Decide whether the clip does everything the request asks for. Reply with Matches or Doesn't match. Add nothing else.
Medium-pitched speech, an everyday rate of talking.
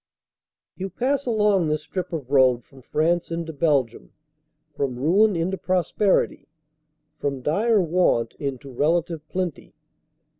Doesn't match